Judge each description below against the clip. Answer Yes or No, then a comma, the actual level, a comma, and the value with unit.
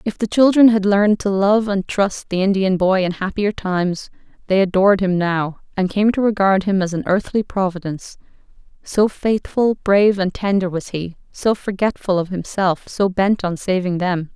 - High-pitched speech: Yes, high, 195 Hz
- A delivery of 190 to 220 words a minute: No, average, 180 wpm